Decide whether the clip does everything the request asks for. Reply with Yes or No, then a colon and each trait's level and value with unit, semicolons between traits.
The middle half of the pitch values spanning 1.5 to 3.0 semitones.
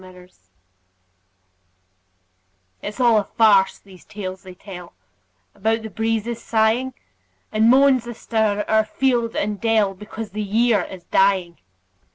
Yes: average, 2.7 semitones